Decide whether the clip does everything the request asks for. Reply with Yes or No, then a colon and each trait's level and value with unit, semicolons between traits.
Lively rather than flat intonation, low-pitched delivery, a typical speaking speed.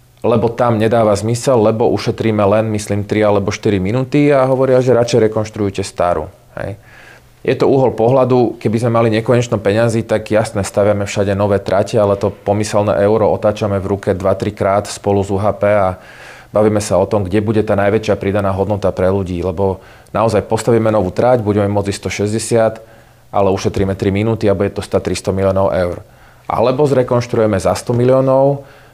No: narrow, 2.6 semitones; low, 105 Hz; average, 170 wpm